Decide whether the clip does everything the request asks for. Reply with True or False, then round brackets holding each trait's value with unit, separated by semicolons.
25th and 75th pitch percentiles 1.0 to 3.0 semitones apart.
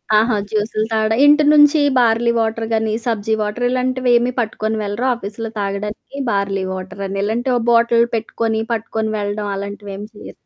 True (2.4 semitones)